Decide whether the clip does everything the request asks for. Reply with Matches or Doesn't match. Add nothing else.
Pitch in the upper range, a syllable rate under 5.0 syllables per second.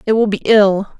Matches